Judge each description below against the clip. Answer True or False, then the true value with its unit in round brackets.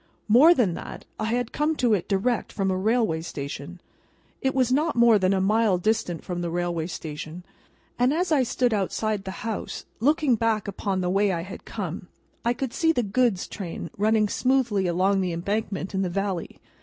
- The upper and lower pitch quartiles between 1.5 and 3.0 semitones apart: False (4.6 semitones)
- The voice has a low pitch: False (205 Hz)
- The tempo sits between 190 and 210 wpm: True (195 wpm)